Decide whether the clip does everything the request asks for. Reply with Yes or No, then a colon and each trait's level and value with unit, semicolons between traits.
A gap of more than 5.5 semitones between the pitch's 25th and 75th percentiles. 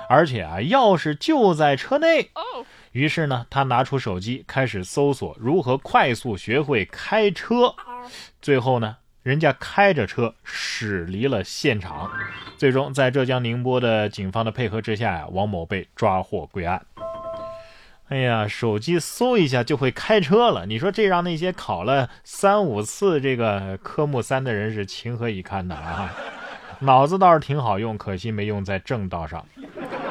Yes: wide, 7.6 semitones